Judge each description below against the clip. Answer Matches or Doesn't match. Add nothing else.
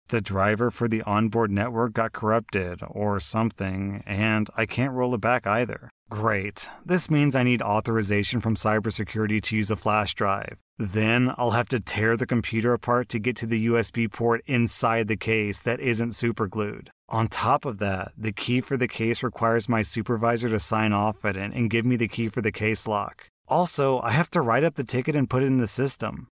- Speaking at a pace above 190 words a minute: Matches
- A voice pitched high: Doesn't match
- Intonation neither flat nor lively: Doesn't match